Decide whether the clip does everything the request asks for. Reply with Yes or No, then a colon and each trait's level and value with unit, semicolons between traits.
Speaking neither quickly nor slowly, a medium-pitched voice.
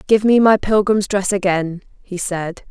No: average, 175 wpm; high, 195 Hz